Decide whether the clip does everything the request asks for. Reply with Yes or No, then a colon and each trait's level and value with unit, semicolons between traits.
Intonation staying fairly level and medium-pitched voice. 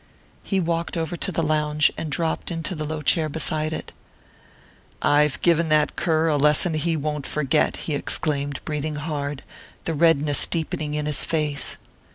Yes: narrow, 1.5 semitones; medium, 155 Hz